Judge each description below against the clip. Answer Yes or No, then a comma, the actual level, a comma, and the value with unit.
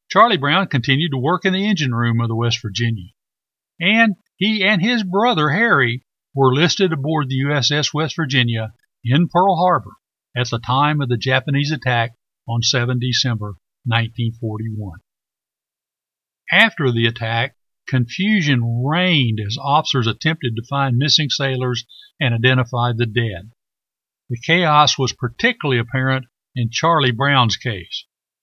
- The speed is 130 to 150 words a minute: Yes, slow, 135 wpm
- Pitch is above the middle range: No, low, 130 Hz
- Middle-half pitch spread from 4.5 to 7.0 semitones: Yes, average, 4.8 semitones